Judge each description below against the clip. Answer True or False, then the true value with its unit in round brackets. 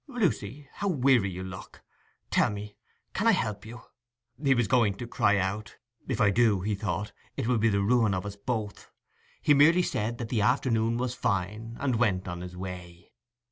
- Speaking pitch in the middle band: False (110 Hz)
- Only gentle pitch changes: False (3.8 semitones)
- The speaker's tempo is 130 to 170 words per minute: False (185 wpm)